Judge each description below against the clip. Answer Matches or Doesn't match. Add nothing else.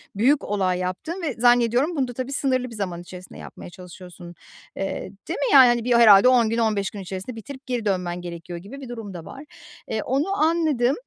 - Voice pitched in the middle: Doesn't match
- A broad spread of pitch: Matches